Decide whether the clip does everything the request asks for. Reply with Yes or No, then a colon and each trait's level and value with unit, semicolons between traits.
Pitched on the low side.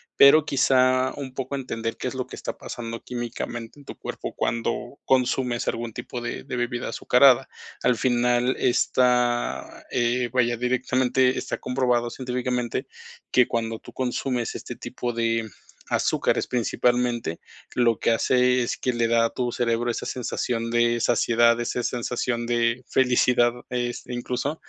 Yes: low, 120 Hz